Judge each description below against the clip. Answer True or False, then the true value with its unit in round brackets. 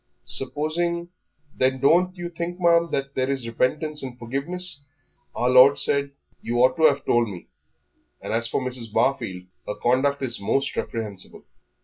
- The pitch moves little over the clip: False (4.4 semitones)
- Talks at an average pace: True (160 wpm)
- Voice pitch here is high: False (135 Hz)